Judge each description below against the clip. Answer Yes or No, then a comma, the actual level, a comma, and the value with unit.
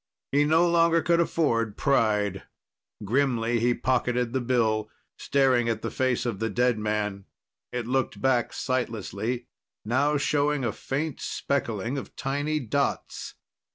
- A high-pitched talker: No, low, 125 Hz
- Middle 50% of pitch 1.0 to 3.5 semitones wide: No, average, 3.9 semitones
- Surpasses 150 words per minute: No, slow, 135 wpm